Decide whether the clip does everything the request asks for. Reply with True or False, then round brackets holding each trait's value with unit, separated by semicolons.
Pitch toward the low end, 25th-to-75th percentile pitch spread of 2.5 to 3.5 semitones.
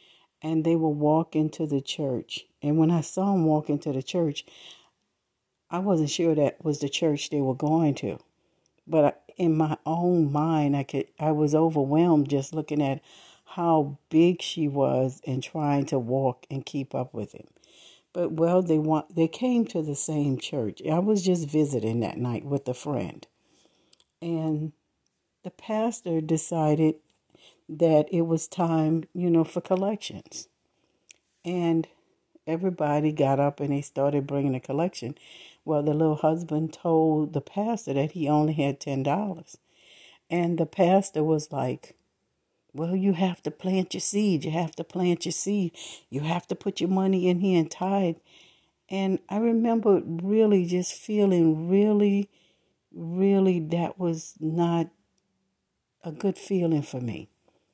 False (160 Hz; 3.1 semitones)